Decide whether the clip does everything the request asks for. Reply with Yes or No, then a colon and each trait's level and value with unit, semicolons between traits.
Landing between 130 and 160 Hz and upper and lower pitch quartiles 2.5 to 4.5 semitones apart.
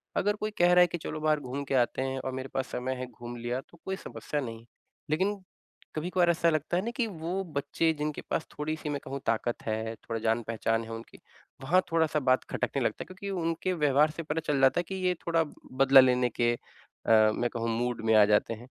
No: medium, 140 Hz; wide, 5.5 semitones